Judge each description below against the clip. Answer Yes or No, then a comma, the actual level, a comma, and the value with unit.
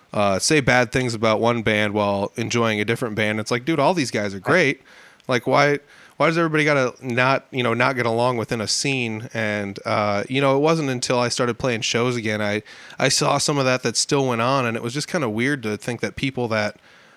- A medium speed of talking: No, fast, 240 wpm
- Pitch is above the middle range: No, low, 120 Hz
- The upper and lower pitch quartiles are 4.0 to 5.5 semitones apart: No, average, 3.6 semitones